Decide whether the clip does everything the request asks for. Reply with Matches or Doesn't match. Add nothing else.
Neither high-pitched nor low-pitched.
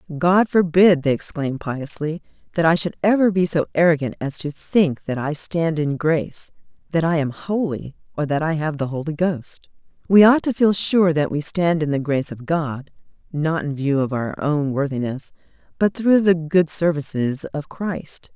Matches